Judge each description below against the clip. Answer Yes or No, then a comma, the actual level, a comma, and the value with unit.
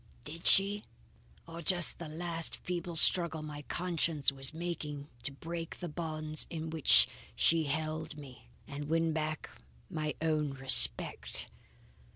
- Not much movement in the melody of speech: Yes, narrow, 2.1 semitones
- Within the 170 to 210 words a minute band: No, slow, 135 wpm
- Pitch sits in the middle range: Yes, medium, 155 Hz